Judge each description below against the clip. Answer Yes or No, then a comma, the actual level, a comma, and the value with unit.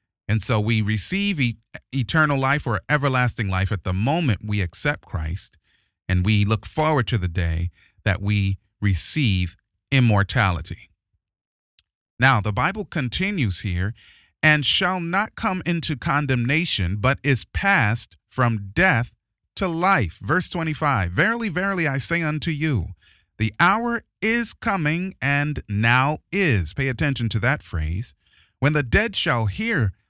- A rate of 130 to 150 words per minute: Yes, average, 140 wpm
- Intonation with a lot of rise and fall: Yes, wide, 7.3 semitones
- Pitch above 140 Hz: No, low, 120 Hz